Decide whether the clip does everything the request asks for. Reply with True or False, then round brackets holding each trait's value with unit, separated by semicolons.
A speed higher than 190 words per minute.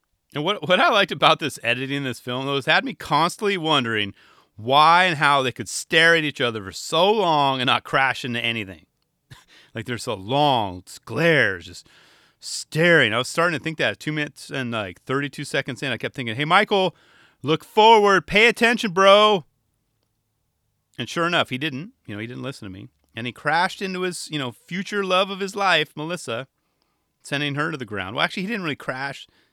True (205 wpm)